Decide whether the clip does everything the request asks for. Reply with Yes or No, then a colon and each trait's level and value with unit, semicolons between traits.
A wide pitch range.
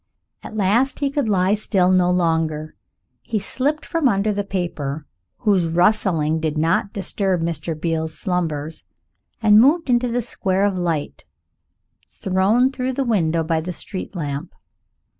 No: average, 4.8 semitones